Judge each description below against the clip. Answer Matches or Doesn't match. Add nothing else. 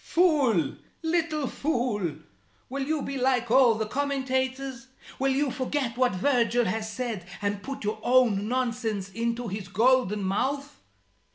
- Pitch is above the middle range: Matches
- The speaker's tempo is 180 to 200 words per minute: Doesn't match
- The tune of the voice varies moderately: Matches